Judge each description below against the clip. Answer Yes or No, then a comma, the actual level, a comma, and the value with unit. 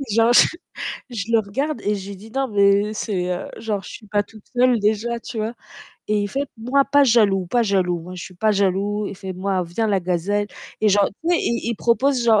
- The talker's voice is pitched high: Yes, high, 210 Hz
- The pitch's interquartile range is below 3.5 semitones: Yes, average, 2.9 semitones